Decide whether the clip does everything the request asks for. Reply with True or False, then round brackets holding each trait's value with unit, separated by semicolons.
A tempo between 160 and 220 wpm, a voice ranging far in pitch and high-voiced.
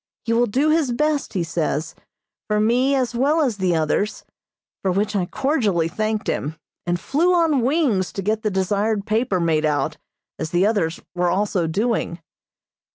True (170 wpm; 6.1 semitones; 210 Hz)